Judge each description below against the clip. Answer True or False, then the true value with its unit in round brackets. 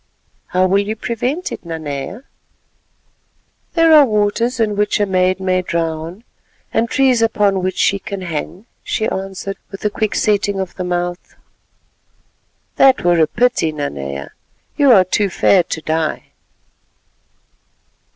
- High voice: True (195 Hz)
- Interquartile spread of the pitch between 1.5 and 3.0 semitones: False (3.8 semitones)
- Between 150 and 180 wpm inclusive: False (140 wpm)